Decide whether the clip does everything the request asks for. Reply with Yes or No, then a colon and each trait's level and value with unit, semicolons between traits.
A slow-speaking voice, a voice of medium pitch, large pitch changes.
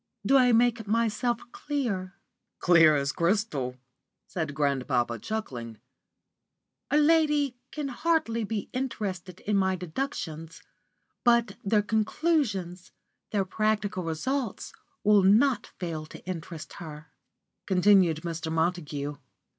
No: slow, 105 wpm; high, 195 Hz; wide, 6.3 semitones